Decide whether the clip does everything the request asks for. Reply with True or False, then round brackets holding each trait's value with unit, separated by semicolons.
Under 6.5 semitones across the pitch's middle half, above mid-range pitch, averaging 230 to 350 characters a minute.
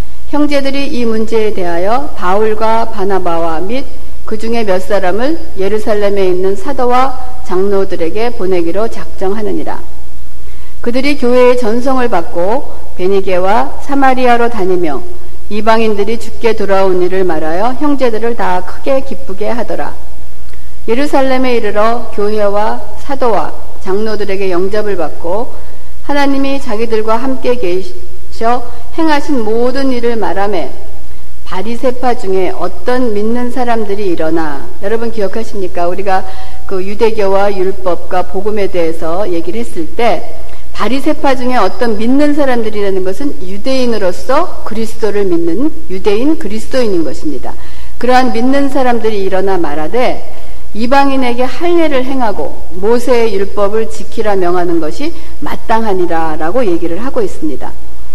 True (5.2 semitones; 220 Hz; 305 characters per minute)